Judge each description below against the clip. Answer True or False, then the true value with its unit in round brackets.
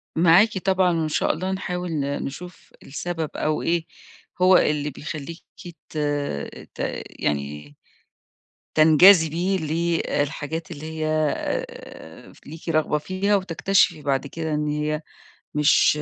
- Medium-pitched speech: True (160 Hz)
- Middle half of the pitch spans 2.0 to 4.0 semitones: True (3.0 semitones)